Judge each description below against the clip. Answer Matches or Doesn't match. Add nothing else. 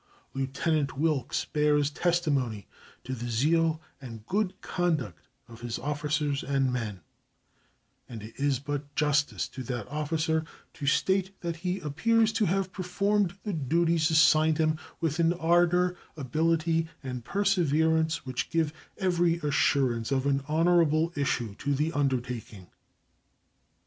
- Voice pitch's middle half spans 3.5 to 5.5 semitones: Matches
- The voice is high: Doesn't match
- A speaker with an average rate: Doesn't match